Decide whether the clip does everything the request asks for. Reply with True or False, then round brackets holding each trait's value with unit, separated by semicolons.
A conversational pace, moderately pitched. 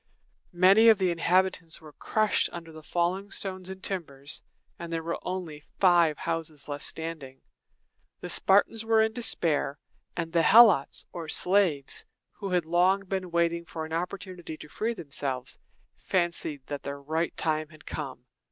True (155 wpm; 170 Hz)